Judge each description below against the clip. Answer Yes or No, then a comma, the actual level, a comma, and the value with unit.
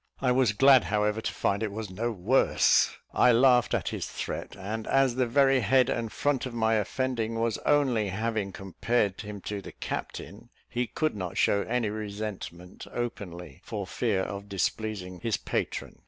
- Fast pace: No, average, 170 wpm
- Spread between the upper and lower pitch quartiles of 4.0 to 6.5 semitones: No, average, 3.5 semitones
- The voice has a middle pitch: No, low, 110 Hz